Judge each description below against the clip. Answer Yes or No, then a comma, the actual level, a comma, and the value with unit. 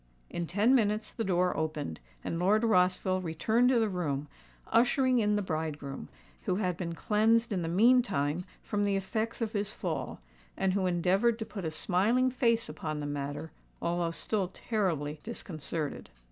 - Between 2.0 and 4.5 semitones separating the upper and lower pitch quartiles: No, average, 5.2 semitones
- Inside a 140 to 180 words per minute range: Yes, average, 165 wpm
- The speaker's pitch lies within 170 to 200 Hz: Yes, medium, 185 Hz